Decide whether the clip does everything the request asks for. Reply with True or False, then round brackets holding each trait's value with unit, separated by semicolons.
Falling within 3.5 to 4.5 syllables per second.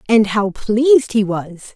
True (4.2 syllables/s)